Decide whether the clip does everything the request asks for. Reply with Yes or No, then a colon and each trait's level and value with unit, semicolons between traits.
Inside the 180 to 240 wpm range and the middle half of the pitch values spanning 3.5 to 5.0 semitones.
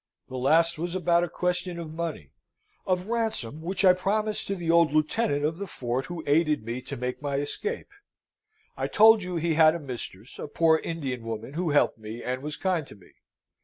Yes: average, 200 wpm; average, 4.7 semitones